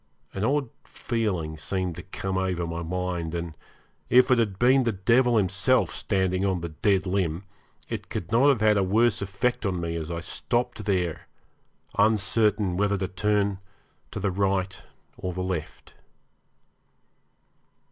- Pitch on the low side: Yes, very low, 95 Hz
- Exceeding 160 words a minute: No, average, 155 wpm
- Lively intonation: No, average, 3.1 semitones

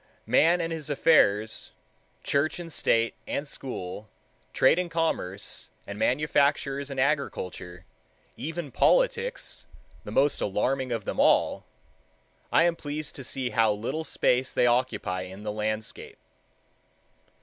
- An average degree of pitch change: No, wide, 6.1 semitones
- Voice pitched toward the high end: No, low, 135 Hz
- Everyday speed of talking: No, slow, 125 wpm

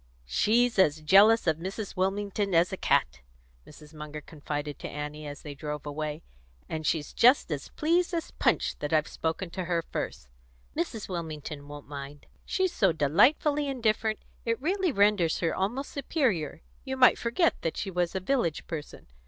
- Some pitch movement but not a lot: No, wide, 7.2 semitones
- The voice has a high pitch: No, medium, 175 Hz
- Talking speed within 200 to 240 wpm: No, average, 170 wpm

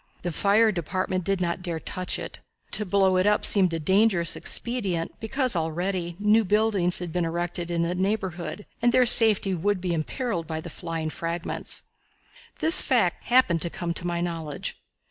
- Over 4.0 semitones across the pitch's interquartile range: No, average, 3.4 semitones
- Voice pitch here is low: No, medium, 180 Hz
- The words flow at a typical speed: Yes, average, 175 wpm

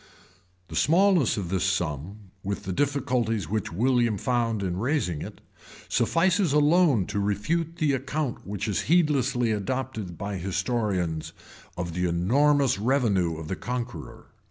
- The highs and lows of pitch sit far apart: Yes, wide, 6.6 semitones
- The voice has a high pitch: No, low, 110 Hz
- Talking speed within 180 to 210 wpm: No, slow, 135 wpm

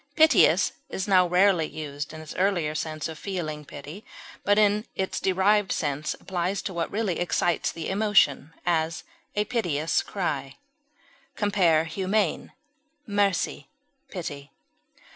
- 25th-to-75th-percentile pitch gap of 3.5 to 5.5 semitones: Yes, average, 4.3 semitones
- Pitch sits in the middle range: Yes, medium, 175 Hz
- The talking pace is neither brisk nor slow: No, slow, 125 wpm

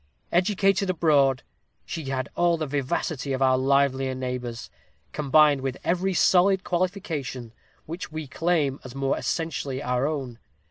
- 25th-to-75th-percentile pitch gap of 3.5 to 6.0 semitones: Yes, average, 4.6 semitones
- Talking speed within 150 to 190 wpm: No, slow, 135 wpm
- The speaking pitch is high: No, medium, 140 Hz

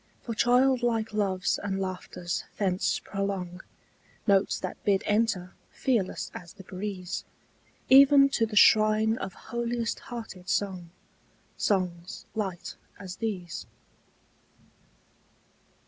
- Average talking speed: No, slow, 100 wpm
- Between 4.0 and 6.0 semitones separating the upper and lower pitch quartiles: No, average, 3.6 semitones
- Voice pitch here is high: Yes, high, 200 Hz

